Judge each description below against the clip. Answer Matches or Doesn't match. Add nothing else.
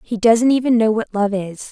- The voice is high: Matches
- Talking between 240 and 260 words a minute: Matches